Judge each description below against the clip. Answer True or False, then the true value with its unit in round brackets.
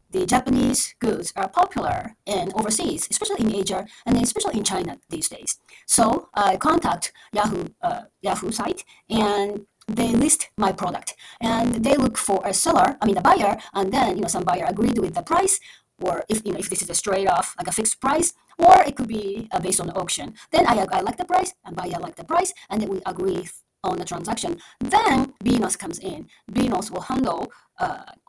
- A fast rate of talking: True (210 wpm)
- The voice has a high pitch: True (240 Hz)